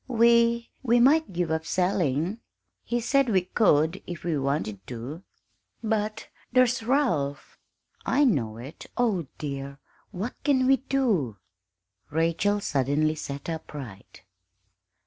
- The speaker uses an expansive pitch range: Yes, wide, 8.6 semitones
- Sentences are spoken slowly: Yes, slow, 120 wpm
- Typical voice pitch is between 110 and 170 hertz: No, medium, 180 Hz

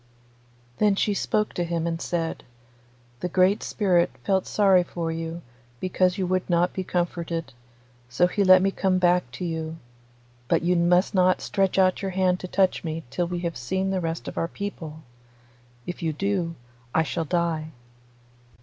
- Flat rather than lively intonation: Yes, narrow, 2.1 semitones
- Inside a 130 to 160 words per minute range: No, average, 175 wpm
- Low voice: No, medium, 180 Hz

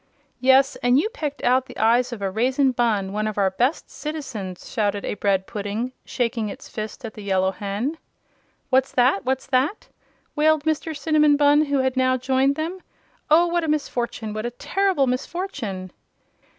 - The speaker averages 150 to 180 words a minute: Yes, average, 175 wpm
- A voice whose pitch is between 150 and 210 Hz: No, very high, 255 Hz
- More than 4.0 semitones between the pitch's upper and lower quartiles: Yes, wide, 5.4 semitones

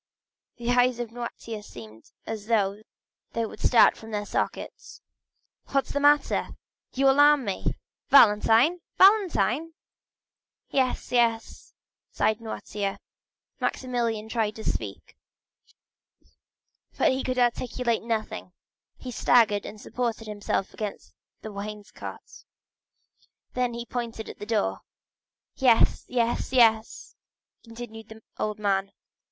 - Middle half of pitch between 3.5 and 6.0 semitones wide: No, average, 2.8 semitones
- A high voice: Yes, high, 230 Hz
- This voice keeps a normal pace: No, slow, 115 wpm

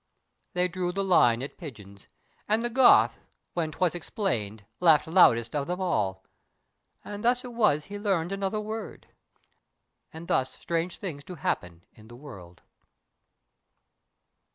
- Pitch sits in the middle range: Yes, medium, 170 Hz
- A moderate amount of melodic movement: No, wide, 8.1 semitones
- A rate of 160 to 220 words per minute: No, average, 140 wpm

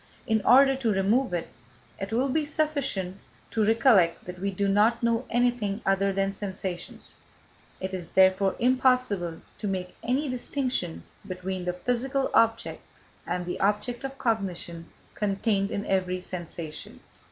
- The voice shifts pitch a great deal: No, average, 4.7 semitones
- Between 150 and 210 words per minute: No, average, 140 wpm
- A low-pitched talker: No, high, 200 Hz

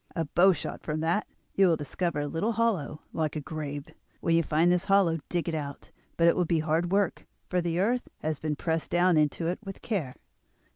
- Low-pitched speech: No, medium, 165 Hz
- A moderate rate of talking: No, fast, 220 wpm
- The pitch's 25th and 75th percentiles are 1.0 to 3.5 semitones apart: Yes, average, 2.9 semitones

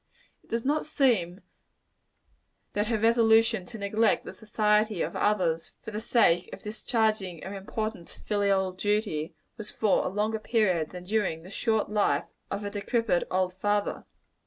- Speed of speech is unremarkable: Yes, average, 160 wpm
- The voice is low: No, high, 210 Hz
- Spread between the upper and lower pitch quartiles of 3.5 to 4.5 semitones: No, average, 2.8 semitones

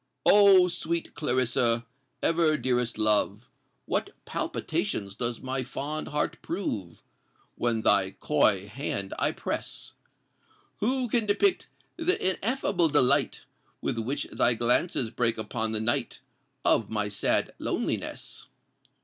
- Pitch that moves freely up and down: Yes, wide, 7.2 semitones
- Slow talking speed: Yes, slow, 115 wpm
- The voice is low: Yes, low, 125 Hz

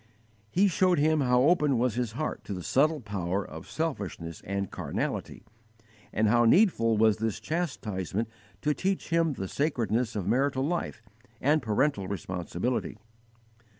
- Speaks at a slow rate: No, average, 145 wpm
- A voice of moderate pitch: No, low, 120 Hz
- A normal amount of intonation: No, wide, 6.8 semitones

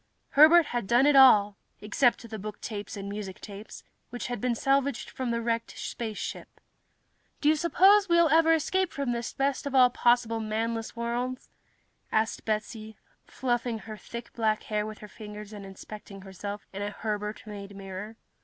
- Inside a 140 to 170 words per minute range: Yes, average, 165 wpm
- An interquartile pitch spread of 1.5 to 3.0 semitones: No, average, 3.5 semitones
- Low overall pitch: No, high, 225 Hz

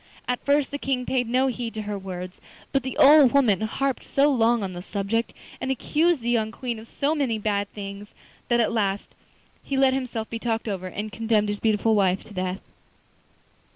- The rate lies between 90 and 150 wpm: No, average, 200 wpm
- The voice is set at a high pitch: Yes, high, 225 Hz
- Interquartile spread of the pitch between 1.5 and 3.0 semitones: No, average, 4.2 semitones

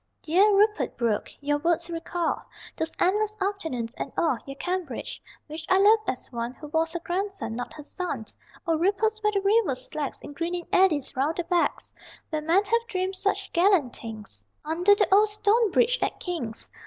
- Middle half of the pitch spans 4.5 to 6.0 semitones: Yes, average, 5.3 semitones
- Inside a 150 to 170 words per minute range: No, average, 180 wpm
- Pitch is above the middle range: Yes, very high, 345 Hz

